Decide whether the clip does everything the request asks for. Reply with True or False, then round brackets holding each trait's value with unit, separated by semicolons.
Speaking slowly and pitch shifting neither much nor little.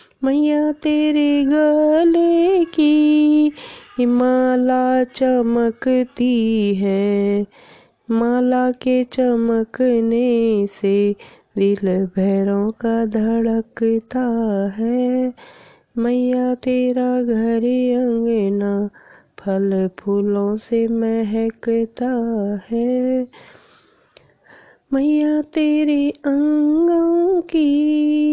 True (60 wpm; 4.4 semitones)